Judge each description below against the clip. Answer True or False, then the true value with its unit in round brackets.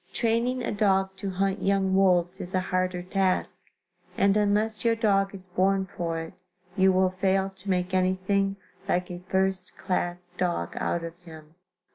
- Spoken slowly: False (165 wpm)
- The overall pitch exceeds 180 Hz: True (190 Hz)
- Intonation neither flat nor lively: False (1.4 semitones)